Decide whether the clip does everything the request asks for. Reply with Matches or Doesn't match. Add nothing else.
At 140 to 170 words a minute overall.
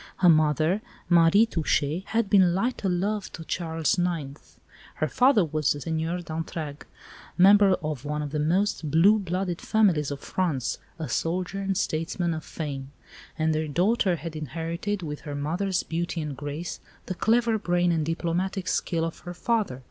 Matches